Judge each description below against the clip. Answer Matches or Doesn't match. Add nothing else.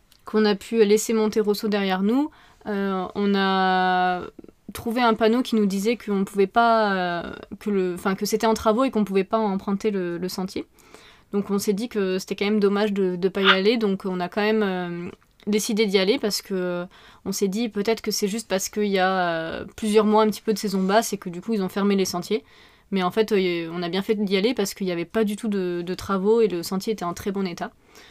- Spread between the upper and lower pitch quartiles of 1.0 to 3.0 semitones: Matches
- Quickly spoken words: Matches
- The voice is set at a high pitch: Matches